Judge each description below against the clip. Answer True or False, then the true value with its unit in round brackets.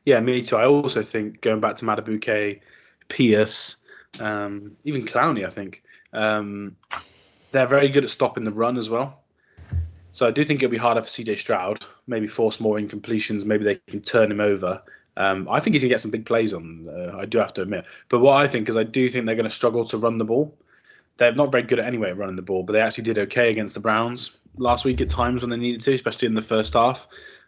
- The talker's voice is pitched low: True (110 Hz)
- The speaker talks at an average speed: False (235 wpm)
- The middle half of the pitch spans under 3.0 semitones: True (2.6 semitones)